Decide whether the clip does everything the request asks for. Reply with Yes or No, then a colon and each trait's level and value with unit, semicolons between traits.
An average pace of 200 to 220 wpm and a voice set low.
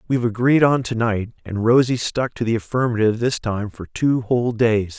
Yes: fast, 205 wpm; low, 115 Hz